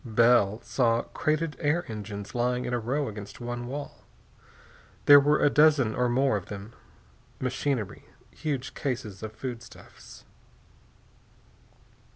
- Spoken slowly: Yes, slow, 125 wpm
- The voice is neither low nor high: No, low, 125 Hz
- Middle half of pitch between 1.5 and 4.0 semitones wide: No, average, 4.4 semitones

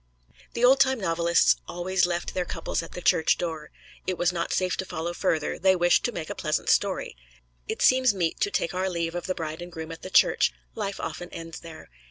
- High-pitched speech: No, medium, 175 Hz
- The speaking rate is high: Yes, fast, 225 wpm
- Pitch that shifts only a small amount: Yes, narrow, 2.2 semitones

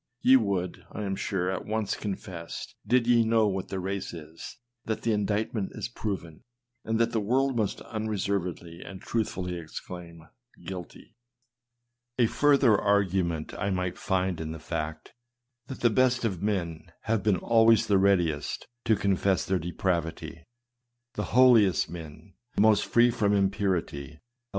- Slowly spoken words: Yes, slow, 130 wpm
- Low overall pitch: Yes, very low, 95 Hz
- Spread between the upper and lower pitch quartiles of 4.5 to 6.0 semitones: No, average, 4.0 semitones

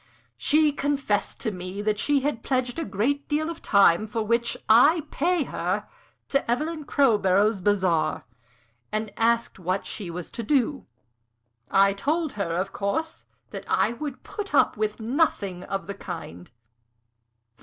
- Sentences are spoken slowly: No, average, 155 wpm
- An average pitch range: No, wide, 6.4 semitones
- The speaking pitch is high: Yes, high, 225 Hz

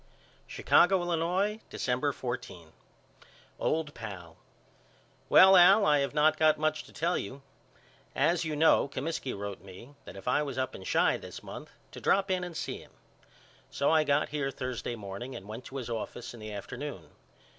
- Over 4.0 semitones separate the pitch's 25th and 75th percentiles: Yes, wide, 5.5 semitones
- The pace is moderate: Yes, average, 175 wpm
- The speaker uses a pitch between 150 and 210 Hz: No, medium, 140 Hz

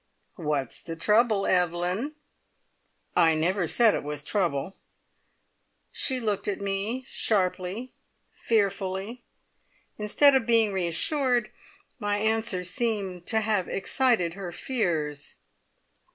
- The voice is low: No, high, 200 Hz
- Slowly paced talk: Yes, slow, 105 wpm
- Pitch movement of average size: Yes, average, 4.2 semitones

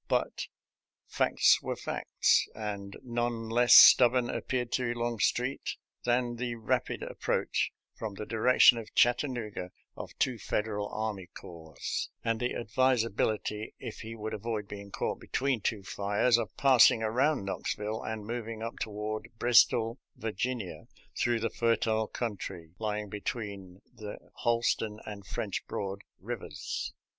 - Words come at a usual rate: No, slow, 130 wpm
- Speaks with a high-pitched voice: No, low, 110 Hz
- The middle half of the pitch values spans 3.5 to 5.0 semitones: No, narrow, 2.5 semitones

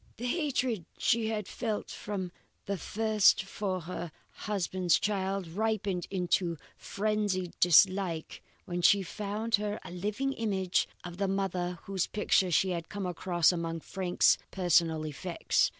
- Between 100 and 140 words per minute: Yes, slow, 135 wpm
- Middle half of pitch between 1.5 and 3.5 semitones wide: Yes, average, 2.9 semitones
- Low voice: No, high, 190 Hz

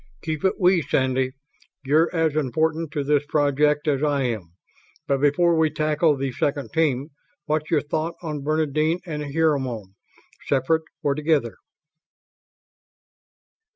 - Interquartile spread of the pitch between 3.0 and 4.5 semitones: No, narrow, 2.4 semitones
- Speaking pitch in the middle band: Yes, medium, 150 Hz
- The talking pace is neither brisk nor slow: No, slow, 130 wpm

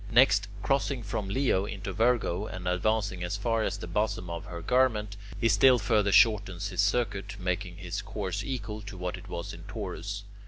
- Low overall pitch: Yes, low, 100 Hz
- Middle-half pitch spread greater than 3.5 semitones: No, average, 3.0 semitones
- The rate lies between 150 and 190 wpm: Yes, average, 185 wpm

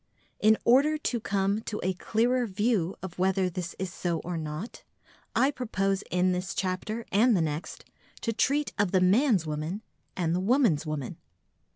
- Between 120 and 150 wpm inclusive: No, average, 170 wpm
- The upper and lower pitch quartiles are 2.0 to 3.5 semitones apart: No, average, 4.3 semitones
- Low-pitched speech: No, high, 190 Hz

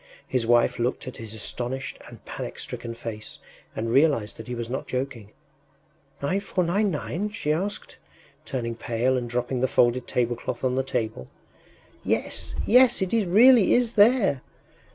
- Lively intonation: Yes, wide, 8.1 semitones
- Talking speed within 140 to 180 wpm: Yes, average, 145 wpm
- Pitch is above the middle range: No, low, 130 Hz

